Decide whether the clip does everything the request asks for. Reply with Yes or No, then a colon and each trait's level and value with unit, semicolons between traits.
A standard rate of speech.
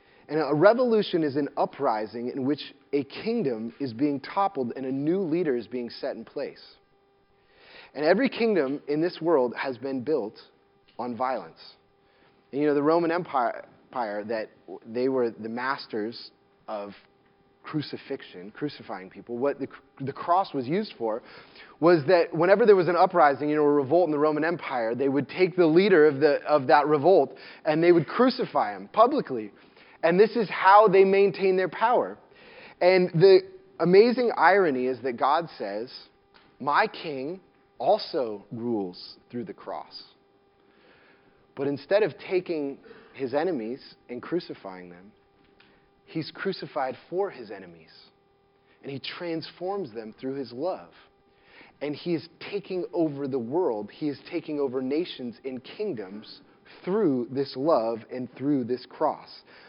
Yes: average, 150 wpm